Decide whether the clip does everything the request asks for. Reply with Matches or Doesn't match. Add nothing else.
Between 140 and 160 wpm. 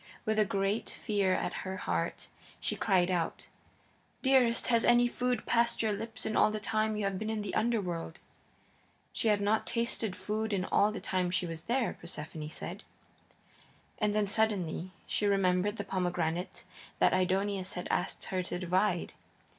Doesn't match